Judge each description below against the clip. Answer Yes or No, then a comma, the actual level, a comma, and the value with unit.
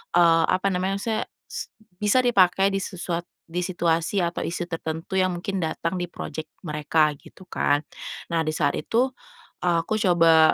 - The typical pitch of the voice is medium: Yes, medium, 175 Hz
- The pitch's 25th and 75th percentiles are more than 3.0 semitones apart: No, average, 2.7 semitones